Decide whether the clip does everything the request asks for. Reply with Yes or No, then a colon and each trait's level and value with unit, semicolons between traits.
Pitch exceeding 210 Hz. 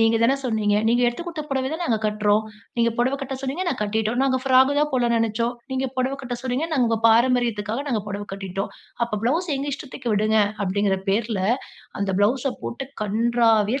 Yes: high, 235 Hz